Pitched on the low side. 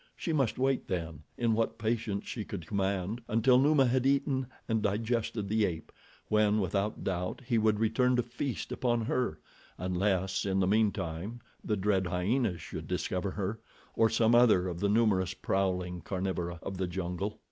Yes: low, 105 Hz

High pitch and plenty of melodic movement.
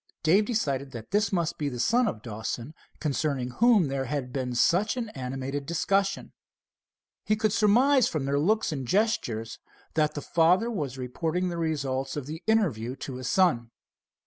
No: medium, 155 Hz; wide, 7.2 semitones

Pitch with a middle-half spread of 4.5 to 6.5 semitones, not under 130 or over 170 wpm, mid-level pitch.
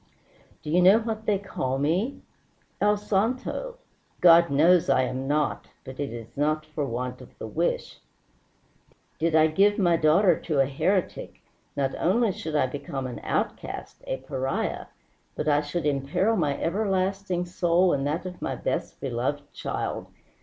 Yes: wide, 5.4 semitones; average, 160 wpm; medium, 160 Hz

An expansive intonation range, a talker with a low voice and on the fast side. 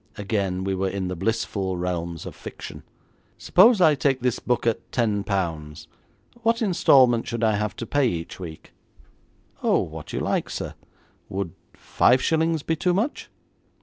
No: wide, 6.7 semitones; low, 110 Hz; average, 160 wpm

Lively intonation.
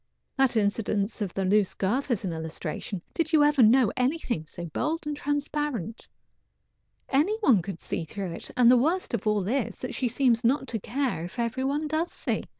Yes: wide, 6.1 semitones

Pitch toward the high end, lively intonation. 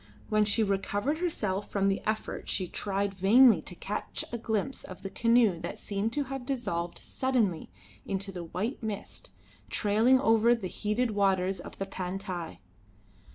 No: high, 205 Hz; average, 3.3 semitones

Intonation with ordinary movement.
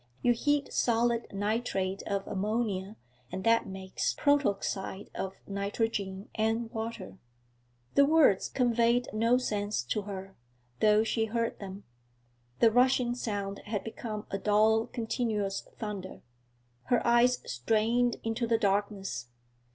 Yes: average, 3.1 semitones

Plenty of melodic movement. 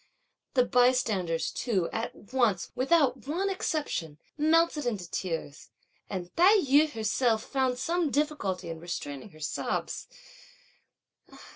Yes: wide, 8.4 semitones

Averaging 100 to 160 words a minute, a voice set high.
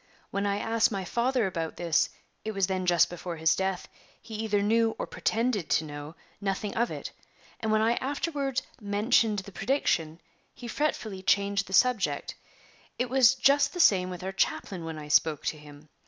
No: average, 185 wpm; high, 200 Hz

